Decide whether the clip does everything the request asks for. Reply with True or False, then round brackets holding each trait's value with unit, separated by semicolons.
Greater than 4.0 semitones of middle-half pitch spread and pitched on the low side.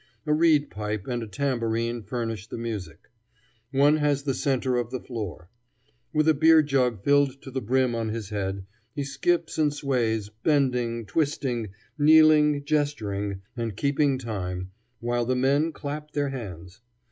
True (4.6 semitones; 130 Hz)